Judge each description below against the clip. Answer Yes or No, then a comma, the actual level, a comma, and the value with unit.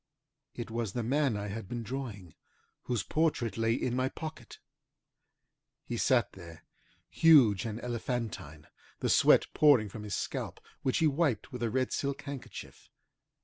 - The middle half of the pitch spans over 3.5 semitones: Yes, average, 3.9 semitones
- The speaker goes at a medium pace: Yes, average, 150 wpm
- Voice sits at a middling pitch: No, low, 120 Hz